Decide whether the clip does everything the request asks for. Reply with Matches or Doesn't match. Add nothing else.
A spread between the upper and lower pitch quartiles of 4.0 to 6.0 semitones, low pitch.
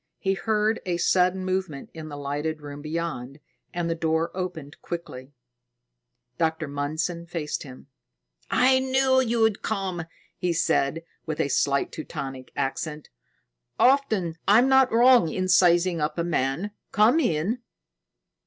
Doesn't match